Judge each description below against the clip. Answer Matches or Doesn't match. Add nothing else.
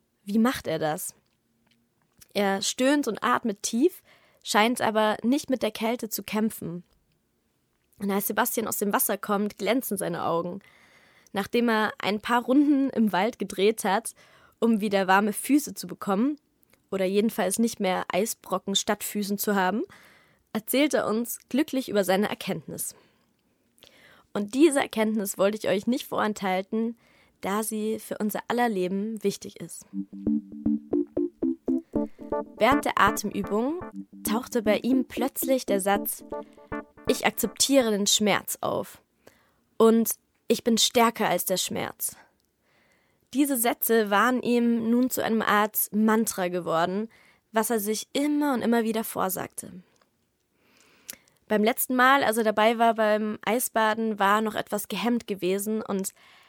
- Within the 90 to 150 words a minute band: Matches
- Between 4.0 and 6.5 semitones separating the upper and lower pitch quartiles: Doesn't match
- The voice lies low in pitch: Doesn't match